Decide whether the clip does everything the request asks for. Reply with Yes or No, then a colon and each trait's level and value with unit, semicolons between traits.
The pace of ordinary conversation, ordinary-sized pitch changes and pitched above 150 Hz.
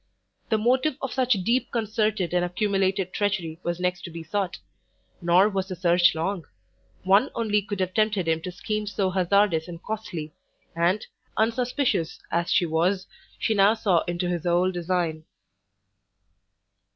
Yes: average, 150 wpm; average, 3.6 semitones; medium, 185 Hz